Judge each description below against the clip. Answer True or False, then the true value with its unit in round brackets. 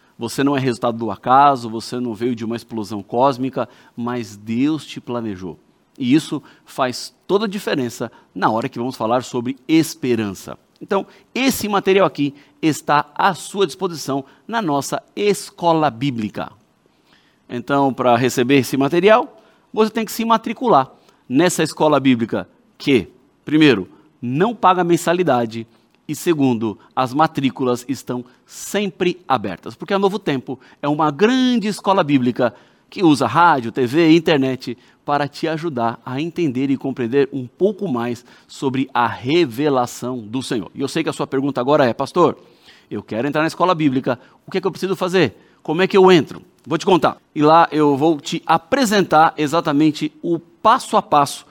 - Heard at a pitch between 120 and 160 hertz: True (140 Hz)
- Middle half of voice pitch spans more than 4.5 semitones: True (5.5 semitones)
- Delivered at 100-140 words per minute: False (160 wpm)